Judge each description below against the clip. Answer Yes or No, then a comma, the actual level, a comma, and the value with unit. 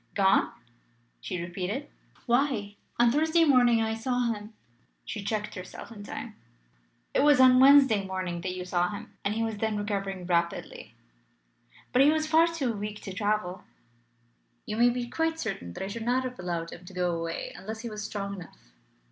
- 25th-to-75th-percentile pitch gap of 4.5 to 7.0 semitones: Yes, average, 4.9 semitones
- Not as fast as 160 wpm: No, average, 185 wpm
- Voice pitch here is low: No, high, 210 Hz